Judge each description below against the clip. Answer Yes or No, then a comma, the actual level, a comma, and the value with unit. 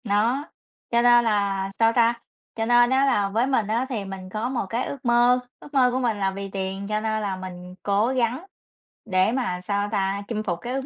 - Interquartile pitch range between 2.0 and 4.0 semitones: Yes, average, 3.5 semitones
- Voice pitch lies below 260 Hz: Yes, high, 220 Hz